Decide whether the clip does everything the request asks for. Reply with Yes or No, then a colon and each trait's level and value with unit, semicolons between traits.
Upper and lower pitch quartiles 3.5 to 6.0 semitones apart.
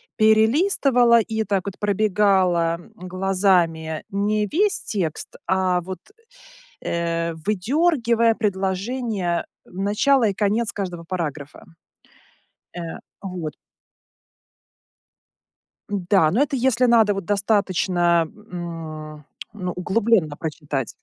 Yes: average, 4.3 semitones